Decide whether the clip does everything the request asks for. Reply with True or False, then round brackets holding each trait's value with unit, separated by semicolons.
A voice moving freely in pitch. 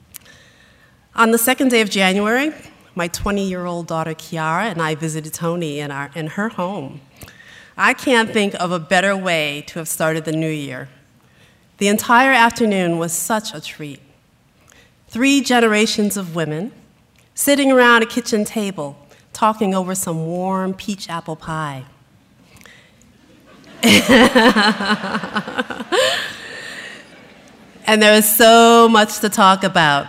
True (5.9 semitones)